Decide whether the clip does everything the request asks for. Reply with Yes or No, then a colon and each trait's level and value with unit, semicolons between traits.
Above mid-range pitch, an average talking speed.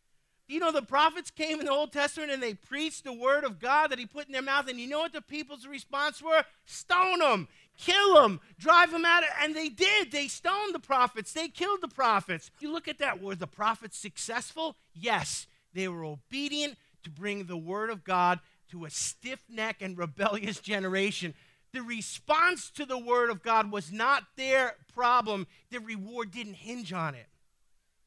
Yes: very high, 250 Hz; average, 190 wpm